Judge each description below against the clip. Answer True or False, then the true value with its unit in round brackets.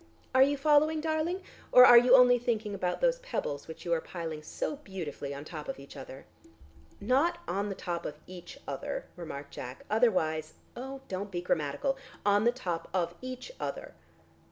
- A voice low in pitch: False (205 Hz)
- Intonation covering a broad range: True (8.2 semitones)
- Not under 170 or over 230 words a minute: True (185 wpm)